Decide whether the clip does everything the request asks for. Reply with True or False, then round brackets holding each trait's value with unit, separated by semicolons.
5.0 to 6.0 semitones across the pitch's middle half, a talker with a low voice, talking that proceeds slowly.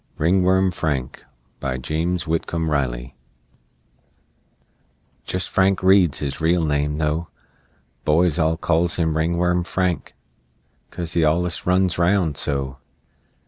False (2.9 semitones; 85 Hz; 110 wpm)